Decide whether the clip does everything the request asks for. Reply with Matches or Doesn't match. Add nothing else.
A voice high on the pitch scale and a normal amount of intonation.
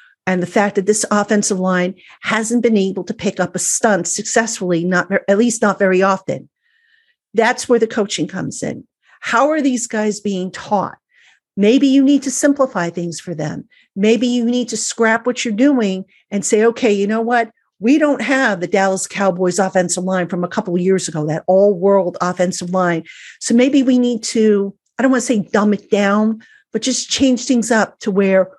Matches